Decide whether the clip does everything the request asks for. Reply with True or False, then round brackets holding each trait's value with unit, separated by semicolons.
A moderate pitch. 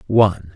False (95 Hz)